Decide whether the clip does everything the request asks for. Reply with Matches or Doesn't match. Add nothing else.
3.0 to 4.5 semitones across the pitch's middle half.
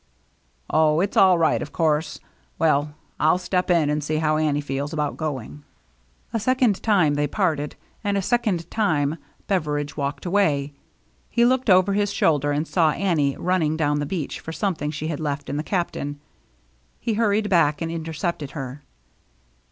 Matches